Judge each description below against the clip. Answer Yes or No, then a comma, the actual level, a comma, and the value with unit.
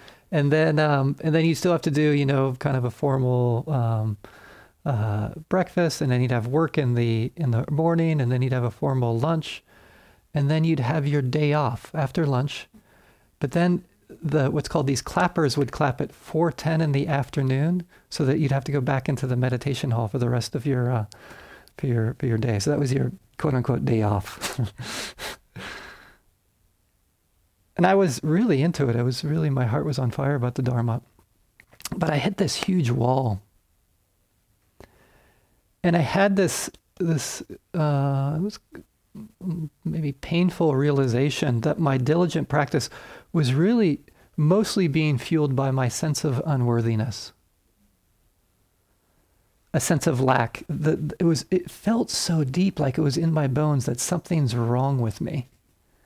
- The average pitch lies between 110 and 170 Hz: Yes, medium, 140 Hz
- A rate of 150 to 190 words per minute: Yes, average, 170 wpm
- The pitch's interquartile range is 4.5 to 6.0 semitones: Yes, average, 4.9 semitones